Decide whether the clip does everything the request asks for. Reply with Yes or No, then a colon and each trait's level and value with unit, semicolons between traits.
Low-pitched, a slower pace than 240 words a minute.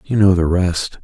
Yes: very low, 90 Hz; fast, 230 wpm